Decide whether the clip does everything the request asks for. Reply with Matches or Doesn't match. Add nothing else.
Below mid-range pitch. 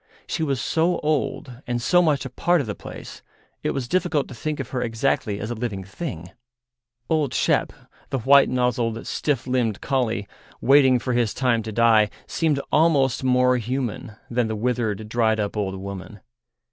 Matches